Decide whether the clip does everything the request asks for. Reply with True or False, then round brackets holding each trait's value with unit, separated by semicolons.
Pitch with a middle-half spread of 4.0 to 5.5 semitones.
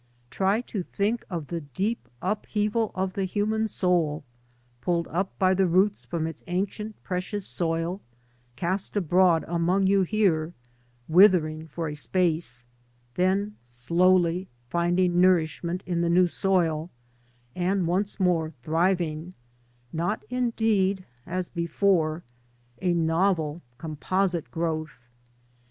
False (3.0 semitones)